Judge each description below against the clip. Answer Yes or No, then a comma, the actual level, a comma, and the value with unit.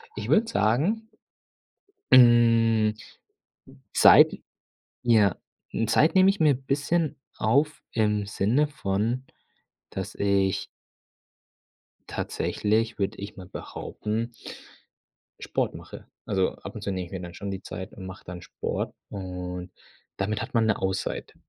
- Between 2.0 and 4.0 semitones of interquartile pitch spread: No, average, 4.7 semitones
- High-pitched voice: No, low, 110 Hz